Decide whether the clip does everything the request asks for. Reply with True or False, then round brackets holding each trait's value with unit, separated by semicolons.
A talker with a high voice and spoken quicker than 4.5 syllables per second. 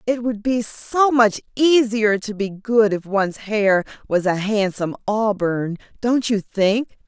False (215 Hz; 3.9 syllables/s)